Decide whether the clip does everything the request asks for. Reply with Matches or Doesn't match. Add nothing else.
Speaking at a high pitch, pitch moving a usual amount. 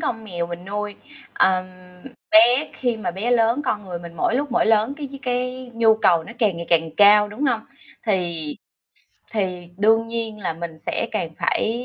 Matches